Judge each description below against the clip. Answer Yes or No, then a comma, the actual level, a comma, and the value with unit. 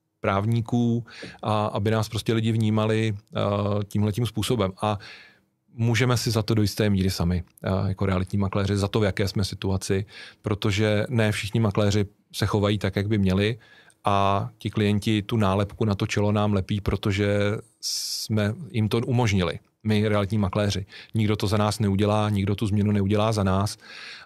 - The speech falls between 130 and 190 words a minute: Yes, average, 165 wpm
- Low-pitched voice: Yes, low, 105 Hz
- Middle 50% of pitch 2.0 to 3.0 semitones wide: No, narrow, 1.4 semitones